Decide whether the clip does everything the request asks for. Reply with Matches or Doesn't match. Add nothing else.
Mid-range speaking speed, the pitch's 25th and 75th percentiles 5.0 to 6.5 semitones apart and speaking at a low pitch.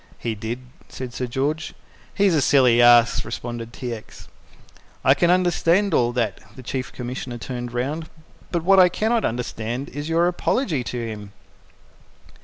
Matches